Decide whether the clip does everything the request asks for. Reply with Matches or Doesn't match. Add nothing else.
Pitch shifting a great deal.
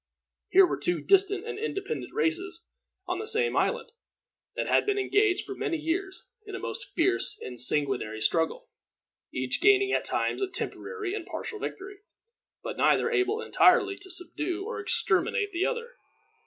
Doesn't match